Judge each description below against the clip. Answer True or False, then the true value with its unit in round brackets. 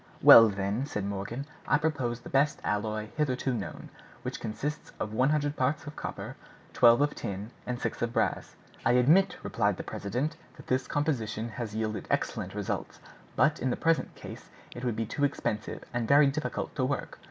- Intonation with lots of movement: False (4.9 semitones)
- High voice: False (125 Hz)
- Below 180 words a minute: False (185 wpm)